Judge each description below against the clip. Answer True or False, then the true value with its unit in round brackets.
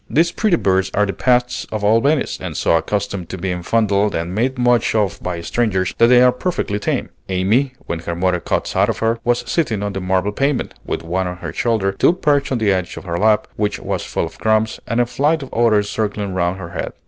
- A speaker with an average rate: False (235 wpm)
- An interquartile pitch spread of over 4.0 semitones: True (4.5 semitones)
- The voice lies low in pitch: True (105 Hz)